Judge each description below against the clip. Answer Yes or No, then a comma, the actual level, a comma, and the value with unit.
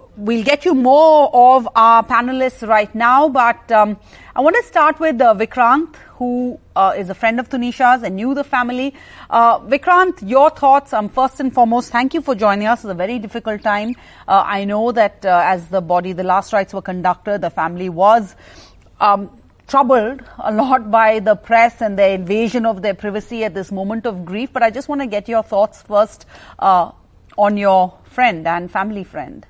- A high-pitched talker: Yes, high, 225 Hz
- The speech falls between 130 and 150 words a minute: No, average, 195 wpm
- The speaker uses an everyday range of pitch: Yes, average, 3.9 semitones